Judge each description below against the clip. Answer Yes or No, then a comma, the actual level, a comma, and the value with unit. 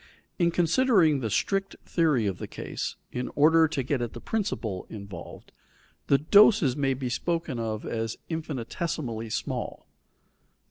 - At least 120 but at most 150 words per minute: Yes, average, 140 wpm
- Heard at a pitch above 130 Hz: Yes, medium, 140 Hz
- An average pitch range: No, wide, 6.4 semitones